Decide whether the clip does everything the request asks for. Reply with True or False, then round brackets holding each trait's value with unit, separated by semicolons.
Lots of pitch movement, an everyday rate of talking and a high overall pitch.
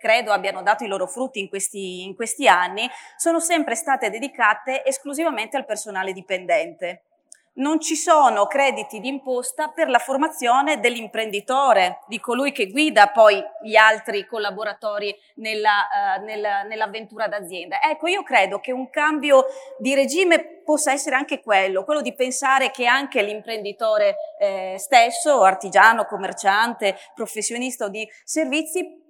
True (6.2 semitones; 135 wpm; 240 Hz)